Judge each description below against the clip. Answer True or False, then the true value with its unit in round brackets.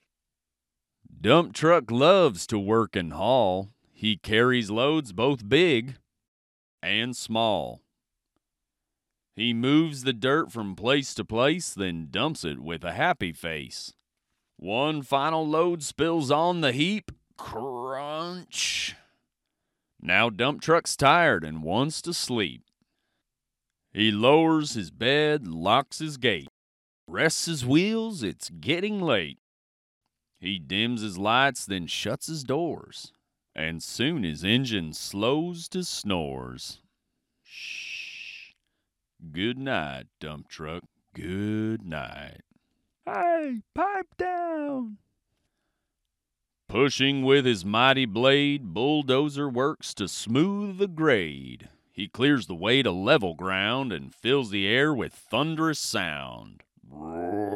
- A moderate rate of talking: False (115 wpm)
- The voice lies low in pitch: True (125 Hz)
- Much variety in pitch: True (8.4 semitones)